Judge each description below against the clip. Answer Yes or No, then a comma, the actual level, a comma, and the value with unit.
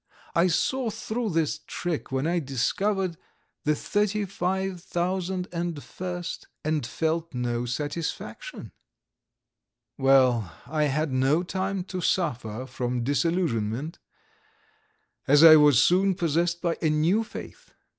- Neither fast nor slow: No, slow, 110 wpm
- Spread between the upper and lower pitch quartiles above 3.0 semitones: Yes, average, 5.1 semitones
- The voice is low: No, medium, 165 Hz